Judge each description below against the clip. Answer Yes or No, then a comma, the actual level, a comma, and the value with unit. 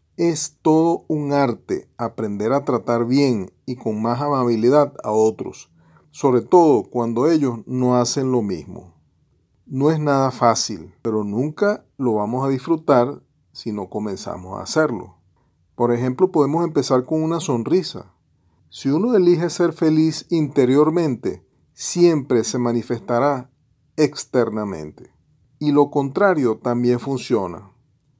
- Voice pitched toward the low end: Yes, low, 130 Hz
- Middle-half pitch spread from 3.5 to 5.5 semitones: Yes, average, 4.2 semitones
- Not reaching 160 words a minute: Yes, slow, 125 wpm